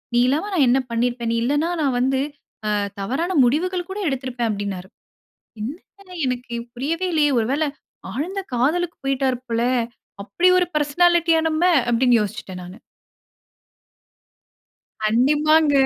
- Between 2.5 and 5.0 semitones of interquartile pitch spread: No, wide, 5.4 semitones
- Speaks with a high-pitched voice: Yes, very high, 270 Hz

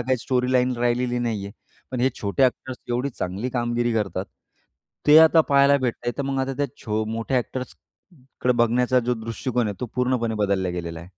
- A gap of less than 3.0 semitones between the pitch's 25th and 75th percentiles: Yes, narrow, 2.4 semitones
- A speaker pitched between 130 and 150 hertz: No, low, 120 Hz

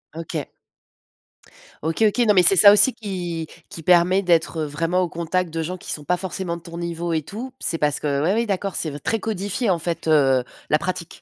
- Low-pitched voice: No, medium, 170 Hz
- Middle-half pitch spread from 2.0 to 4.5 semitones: Yes, average, 2.8 semitones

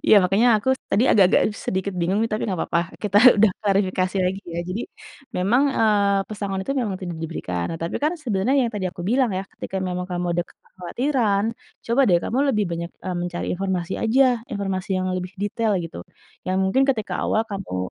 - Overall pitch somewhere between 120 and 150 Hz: No, high, 195 Hz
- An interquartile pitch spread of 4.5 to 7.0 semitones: No, average, 3.2 semitones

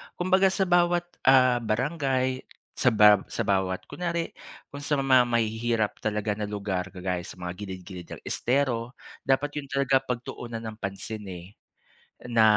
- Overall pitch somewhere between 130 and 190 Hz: No, low, 115 Hz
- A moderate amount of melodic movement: Yes, average, 4.9 semitones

